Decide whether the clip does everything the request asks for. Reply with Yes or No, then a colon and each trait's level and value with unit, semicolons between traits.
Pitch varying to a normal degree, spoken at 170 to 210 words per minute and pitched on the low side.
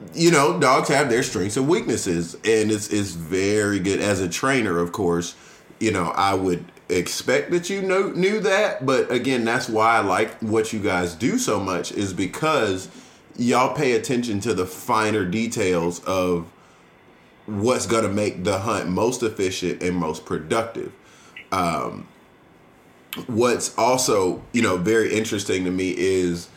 No: average, 4.1 semitones; average, 160 wpm; low, 105 Hz